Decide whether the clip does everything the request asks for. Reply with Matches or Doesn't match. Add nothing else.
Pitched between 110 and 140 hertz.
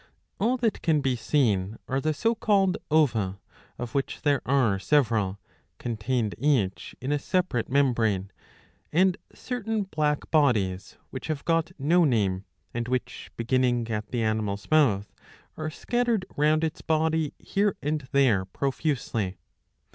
Matches